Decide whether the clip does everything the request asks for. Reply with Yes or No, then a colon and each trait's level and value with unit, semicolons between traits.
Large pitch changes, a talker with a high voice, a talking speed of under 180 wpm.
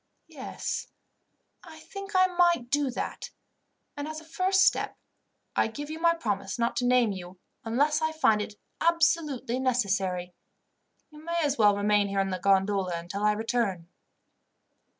Yes: wide, 8.0 semitones; high, 245 Hz; average, 155 wpm